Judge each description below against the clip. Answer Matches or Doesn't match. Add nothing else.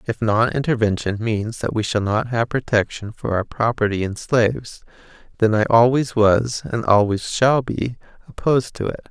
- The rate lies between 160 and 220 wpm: Matches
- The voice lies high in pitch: Doesn't match